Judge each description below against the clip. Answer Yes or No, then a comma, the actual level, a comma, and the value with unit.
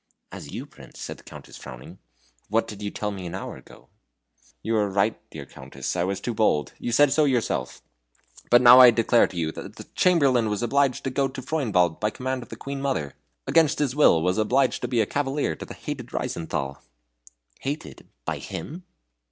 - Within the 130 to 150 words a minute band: No, average, 200 wpm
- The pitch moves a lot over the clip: Yes, wide, 6.9 semitones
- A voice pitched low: Yes, low, 115 Hz